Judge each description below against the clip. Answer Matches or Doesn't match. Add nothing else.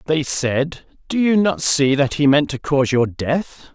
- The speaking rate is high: Matches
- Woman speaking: Doesn't match